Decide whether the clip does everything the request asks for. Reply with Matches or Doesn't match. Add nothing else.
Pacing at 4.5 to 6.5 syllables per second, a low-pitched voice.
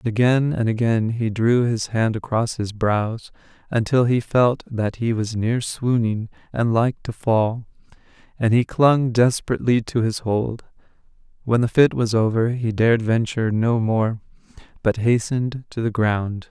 Doesn't match